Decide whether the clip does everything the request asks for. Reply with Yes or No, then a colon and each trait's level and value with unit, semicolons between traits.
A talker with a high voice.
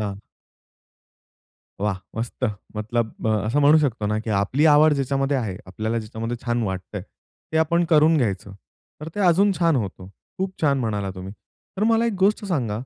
No: low, 120 Hz